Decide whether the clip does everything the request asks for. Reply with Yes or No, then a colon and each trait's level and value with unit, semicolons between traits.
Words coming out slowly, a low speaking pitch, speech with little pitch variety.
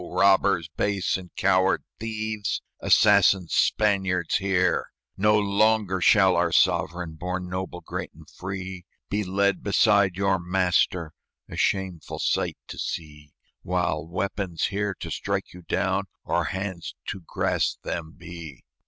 Yes: slow, 130 wpm; very low, 95 Hz; narrow, 2.1 semitones